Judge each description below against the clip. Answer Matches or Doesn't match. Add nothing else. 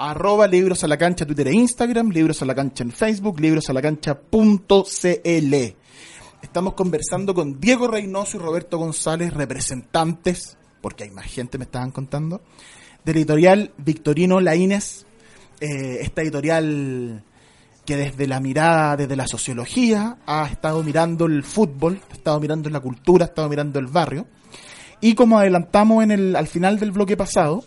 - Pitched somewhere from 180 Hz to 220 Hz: Doesn't match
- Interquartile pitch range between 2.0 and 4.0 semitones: Doesn't match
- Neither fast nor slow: Matches